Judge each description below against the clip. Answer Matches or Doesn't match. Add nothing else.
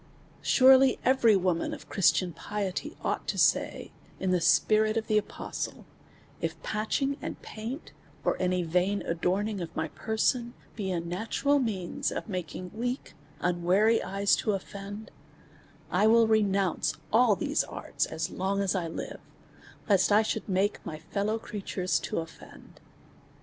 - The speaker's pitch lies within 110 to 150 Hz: Doesn't match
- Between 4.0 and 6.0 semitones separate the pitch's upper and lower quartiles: Doesn't match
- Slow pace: Doesn't match